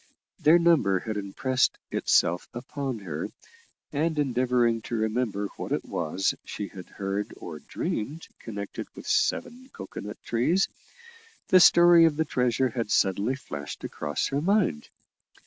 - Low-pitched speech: Yes, low, 120 Hz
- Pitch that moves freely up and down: Yes, wide, 7.6 semitones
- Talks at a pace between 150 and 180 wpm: No, average, 140 wpm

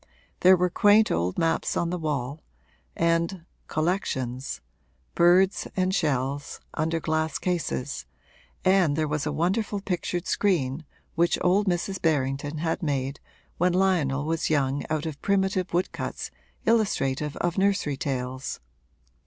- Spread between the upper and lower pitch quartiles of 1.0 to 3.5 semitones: No, average, 4.3 semitones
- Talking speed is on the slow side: Yes, slow, 130 wpm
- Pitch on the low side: No, medium, 165 Hz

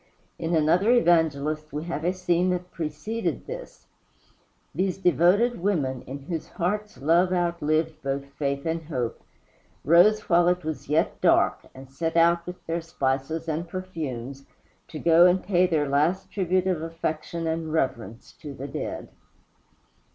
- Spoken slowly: No, average, 150 wpm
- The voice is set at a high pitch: No, medium, 165 Hz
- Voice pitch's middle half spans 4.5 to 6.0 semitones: No, average, 3.2 semitones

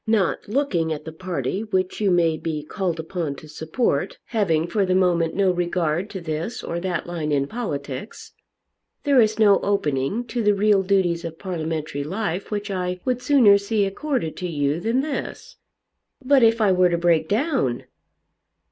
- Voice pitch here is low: No, medium, 185 Hz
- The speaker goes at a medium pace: Yes, average, 175 wpm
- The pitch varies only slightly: No, average, 4.7 semitones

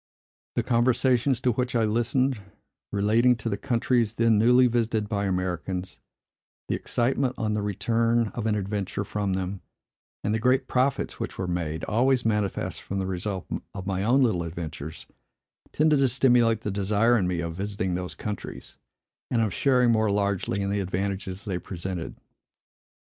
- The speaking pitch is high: No, low, 105 Hz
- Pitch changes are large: No, average, 3.9 semitones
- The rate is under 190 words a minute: Yes, average, 165 wpm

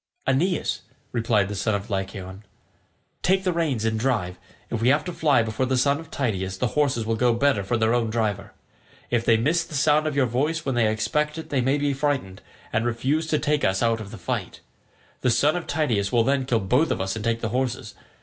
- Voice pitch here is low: Yes, low, 120 Hz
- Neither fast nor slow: No, fast, 225 wpm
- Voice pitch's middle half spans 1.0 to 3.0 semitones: No, average, 4.8 semitones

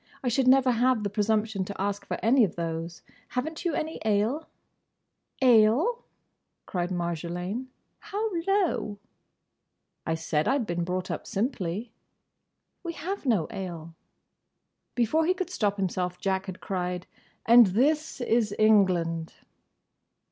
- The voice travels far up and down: Yes, wide, 6.3 semitones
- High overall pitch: Yes, high, 210 Hz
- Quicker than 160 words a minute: No, slow, 135 wpm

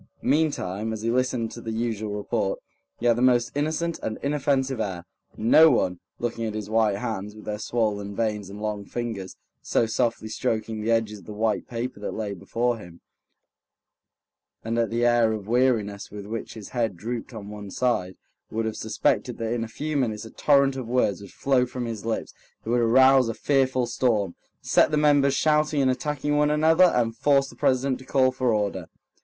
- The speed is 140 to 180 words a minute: No, average, 195 wpm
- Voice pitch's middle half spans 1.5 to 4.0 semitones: Yes, average, 3.4 semitones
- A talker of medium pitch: No, low, 115 Hz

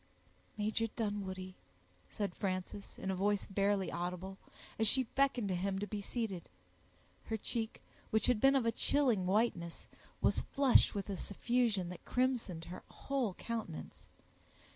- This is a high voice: Yes, high, 205 Hz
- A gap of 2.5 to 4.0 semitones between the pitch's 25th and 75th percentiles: Yes, average, 3.7 semitones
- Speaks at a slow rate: No, average, 145 wpm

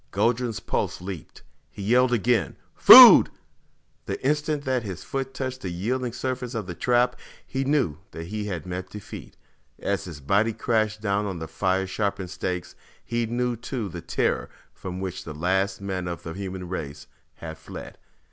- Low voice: Yes, low, 100 Hz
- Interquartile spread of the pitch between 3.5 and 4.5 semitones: No, average, 5.1 semitones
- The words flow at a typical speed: Yes, average, 170 wpm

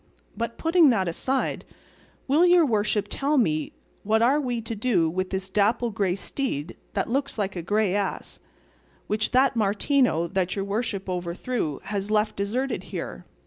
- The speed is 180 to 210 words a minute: No, average, 160 wpm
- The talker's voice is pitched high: Yes, high, 215 Hz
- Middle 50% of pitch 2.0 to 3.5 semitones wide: No, average, 4.8 semitones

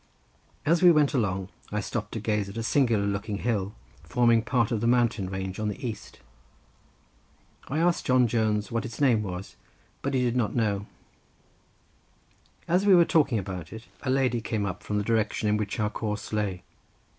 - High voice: No, low, 110 Hz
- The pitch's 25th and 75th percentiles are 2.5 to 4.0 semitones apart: Yes, average, 3.5 semitones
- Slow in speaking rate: No, average, 190 wpm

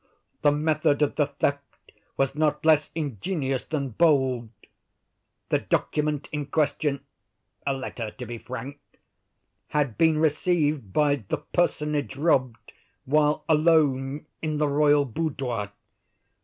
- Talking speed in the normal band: No, slow, 115 wpm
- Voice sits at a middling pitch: Yes, medium, 145 Hz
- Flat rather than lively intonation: Yes, narrow, 2.3 semitones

